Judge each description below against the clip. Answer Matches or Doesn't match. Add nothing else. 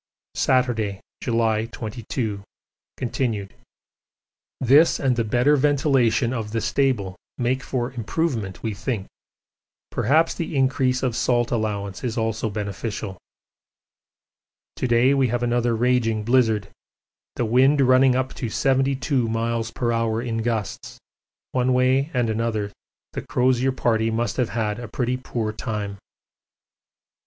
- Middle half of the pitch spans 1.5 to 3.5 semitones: Matches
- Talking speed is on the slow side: Matches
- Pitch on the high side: Doesn't match